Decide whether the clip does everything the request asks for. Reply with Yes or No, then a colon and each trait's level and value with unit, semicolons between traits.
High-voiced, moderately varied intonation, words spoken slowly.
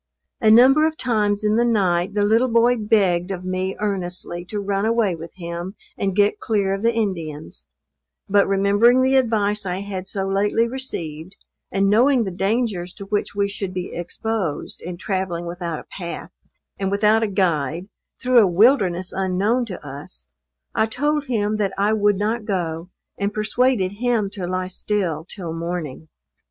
No: high, 200 Hz; average, 3.5 semitones; average, 170 wpm